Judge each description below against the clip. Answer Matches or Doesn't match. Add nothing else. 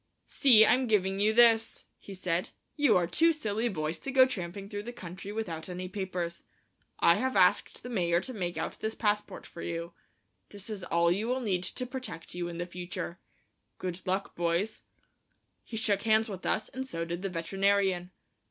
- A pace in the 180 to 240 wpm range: Matches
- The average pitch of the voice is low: Doesn't match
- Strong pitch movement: Doesn't match